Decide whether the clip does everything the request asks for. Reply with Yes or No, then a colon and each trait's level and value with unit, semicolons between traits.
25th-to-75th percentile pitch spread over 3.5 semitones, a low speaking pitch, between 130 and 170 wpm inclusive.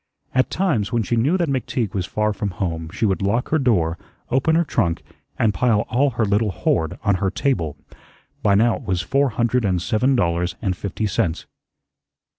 No: average, 5.2 semitones; low, 105 Hz; average, 195 wpm